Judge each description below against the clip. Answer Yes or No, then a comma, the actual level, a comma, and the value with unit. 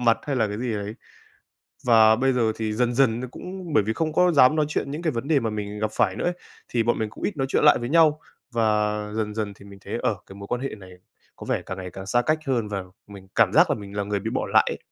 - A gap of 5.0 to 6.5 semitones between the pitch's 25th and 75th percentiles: No, average, 4.6 semitones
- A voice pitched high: No, low, 115 Hz